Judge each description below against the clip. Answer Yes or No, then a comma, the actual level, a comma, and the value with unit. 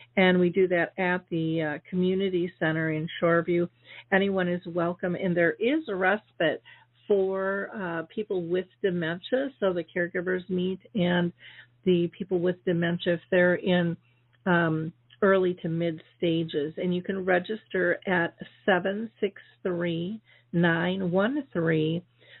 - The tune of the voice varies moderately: No, narrow, 2.1 semitones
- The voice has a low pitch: No, medium, 180 Hz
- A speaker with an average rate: No, slow, 125 wpm